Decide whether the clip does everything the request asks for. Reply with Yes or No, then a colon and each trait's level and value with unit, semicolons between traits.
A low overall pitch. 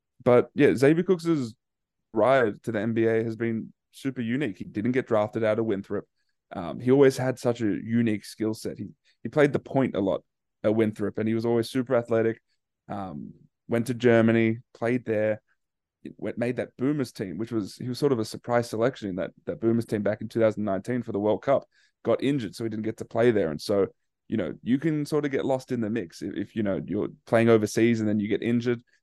Yes: low, 115 Hz